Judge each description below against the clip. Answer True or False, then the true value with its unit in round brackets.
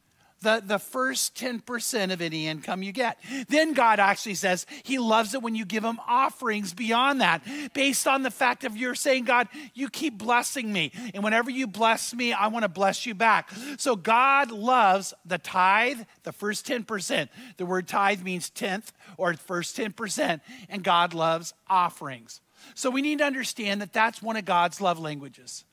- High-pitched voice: True (225 Hz)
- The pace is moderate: True (180 wpm)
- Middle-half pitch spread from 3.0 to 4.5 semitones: False (5.2 semitones)